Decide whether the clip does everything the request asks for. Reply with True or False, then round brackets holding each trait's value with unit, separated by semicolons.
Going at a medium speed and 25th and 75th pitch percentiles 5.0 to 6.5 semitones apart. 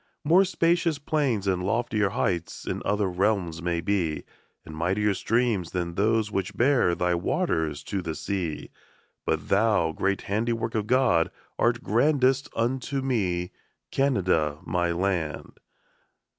False (130 wpm; 5.5 semitones)